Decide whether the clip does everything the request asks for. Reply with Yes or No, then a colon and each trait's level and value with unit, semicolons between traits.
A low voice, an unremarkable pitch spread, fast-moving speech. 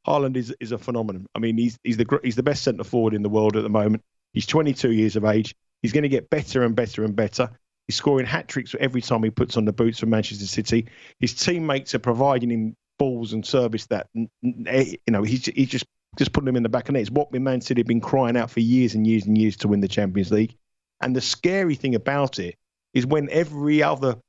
Yes: low, 120 Hz; average, 3.3 semitones; fast, 245 wpm